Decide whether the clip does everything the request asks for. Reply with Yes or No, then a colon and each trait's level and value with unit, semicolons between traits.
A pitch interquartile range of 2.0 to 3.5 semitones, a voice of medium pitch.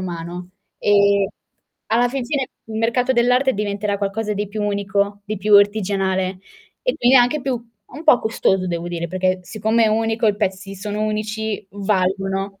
No: narrow, 2.5 semitones; high, 205 Hz